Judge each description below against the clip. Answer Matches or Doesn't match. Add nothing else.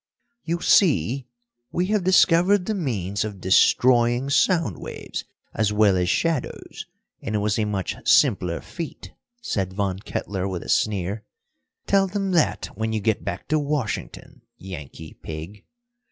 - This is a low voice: Matches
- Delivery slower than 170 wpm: Matches